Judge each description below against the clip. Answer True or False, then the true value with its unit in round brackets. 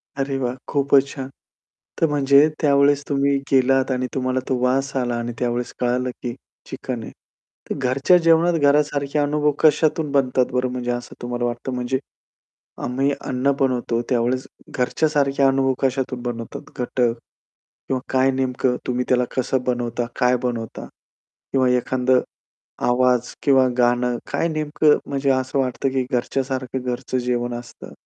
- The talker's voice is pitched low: True (130 Hz)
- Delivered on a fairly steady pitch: True (2.0 semitones)